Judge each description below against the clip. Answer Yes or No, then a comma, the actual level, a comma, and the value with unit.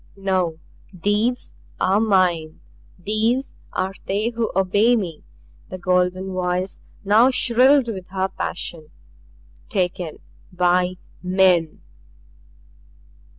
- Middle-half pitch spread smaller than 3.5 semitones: Yes, average, 3.0 semitones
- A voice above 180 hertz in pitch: Yes, high, 190 Hz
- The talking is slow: Yes, slow, 95 wpm